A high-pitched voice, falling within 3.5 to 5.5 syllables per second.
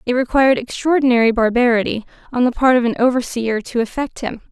No: high, 245 Hz; 6.1 syllables/s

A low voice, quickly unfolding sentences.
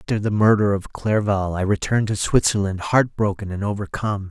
No: low, 100 Hz; average, 180 wpm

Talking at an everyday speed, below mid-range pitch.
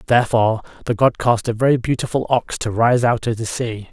No: fast, 215 wpm; low, 115 Hz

